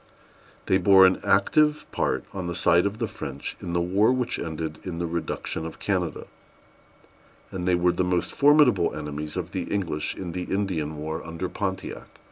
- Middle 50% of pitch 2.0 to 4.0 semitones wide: Yes, average, 2.8 semitones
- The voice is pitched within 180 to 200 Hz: No, very low, 90 Hz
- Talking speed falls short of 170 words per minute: No, average, 180 wpm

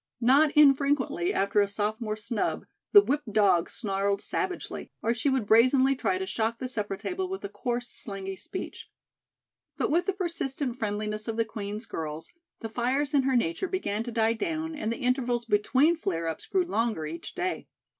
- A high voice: Yes, high, 235 Hz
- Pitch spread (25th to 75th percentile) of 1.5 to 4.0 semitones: No, wide, 5.5 semitones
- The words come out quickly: No, average, 180 wpm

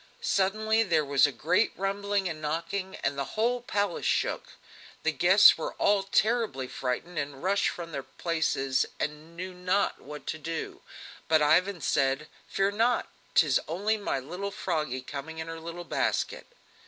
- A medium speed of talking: Yes, average, 155 wpm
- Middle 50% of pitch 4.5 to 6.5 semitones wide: Yes, average, 4.9 semitones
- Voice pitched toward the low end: No, medium, 170 Hz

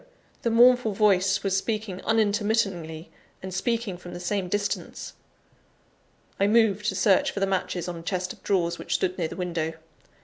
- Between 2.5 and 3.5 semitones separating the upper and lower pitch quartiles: Yes, average, 2.9 semitones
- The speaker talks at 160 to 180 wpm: Yes, average, 170 wpm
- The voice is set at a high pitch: Yes, high, 195 Hz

